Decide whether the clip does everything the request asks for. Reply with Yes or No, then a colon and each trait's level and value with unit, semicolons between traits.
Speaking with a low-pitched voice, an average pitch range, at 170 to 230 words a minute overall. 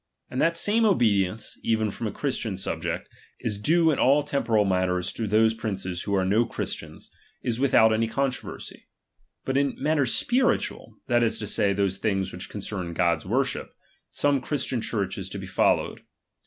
No: low, 110 Hz; wide, 5.7 semitones; average, 180 wpm